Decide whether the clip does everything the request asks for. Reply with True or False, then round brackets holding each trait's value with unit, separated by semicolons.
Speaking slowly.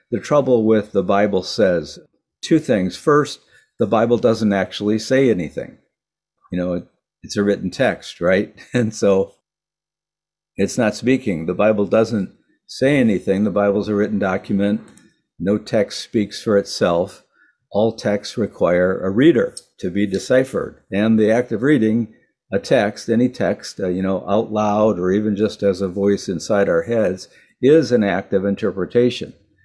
False (160 wpm)